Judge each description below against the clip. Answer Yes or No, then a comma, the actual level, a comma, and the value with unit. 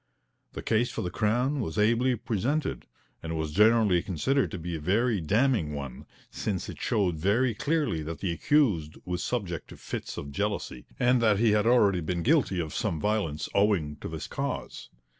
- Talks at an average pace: Yes, average, 180 wpm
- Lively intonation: Yes, wide, 6.2 semitones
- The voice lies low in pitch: Yes, low, 100 Hz